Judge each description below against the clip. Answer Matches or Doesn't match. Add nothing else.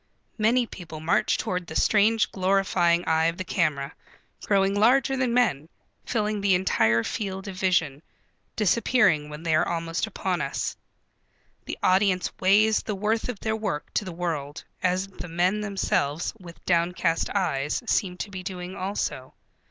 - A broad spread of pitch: Doesn't match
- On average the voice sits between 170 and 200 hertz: Matches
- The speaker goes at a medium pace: Matches